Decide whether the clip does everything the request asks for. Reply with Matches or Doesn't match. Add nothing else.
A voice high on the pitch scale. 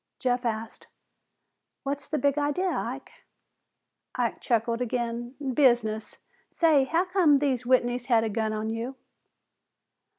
Matches